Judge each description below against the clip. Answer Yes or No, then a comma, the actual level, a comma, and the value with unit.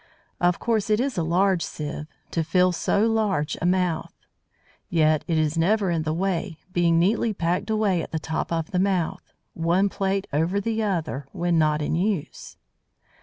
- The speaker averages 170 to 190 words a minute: Yes, average, 175 wpm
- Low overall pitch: No, medium, 175 Hz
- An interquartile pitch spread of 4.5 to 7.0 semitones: No, average, 3.5 semitones